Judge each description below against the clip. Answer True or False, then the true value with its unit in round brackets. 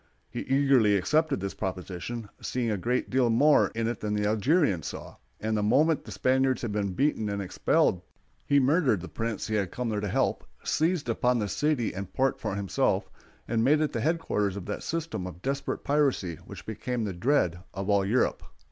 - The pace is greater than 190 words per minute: True (200 wpm)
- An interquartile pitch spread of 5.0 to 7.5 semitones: True (5.3 semitones)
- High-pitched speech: False (115 Hz)